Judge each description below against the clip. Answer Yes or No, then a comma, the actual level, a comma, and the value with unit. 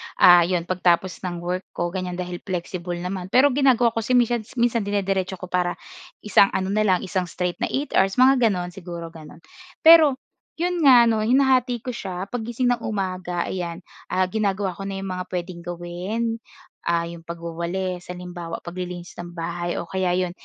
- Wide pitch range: No, average, 4.0 semitones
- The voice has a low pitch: No, medium, 185 Hz